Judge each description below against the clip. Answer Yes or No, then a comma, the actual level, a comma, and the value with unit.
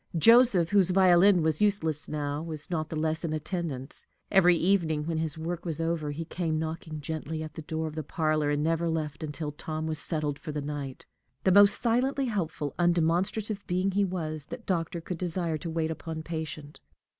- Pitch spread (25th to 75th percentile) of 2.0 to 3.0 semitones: Yes, narrow, 2.5 semitones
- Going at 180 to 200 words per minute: Yes, average, 190 wpm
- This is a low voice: No, medium, 160 Hz